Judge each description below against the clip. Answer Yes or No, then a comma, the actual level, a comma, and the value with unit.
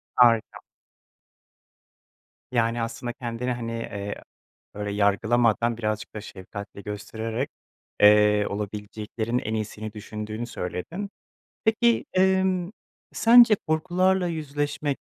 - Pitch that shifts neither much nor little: No, wide, 5.9 semitones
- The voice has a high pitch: No, low, 115 Hz